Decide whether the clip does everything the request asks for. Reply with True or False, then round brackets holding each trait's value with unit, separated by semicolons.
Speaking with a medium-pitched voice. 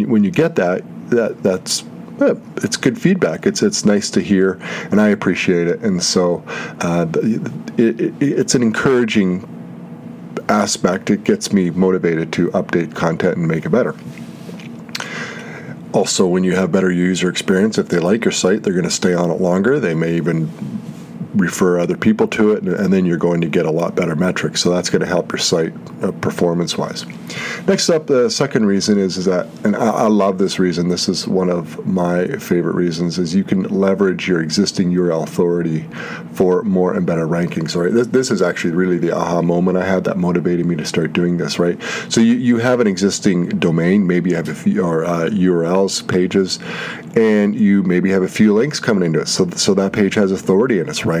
False (90 Hz)